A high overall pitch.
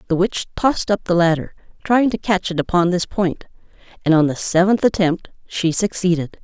No: medium, 180 Hz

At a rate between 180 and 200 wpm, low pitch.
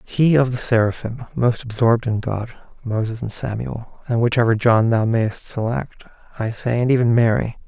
No: average, 170 wpm; low, 115 Hz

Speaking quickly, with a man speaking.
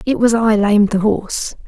No: fast, 215 wpm; female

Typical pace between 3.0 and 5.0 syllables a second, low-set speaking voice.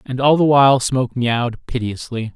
No: 5.5 syllables/s; low, 125 Hz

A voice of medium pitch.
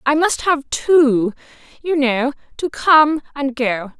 No: very high, 275 Hz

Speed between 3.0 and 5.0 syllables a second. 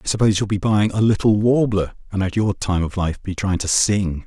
No: 5.5 syllables/s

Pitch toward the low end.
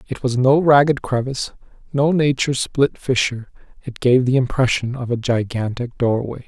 Yes: low, 125 Hz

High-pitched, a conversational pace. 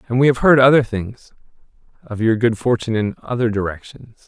No: low, 115 Hz; average, 180 wpm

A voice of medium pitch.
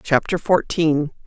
Yes: medium, 160 Hz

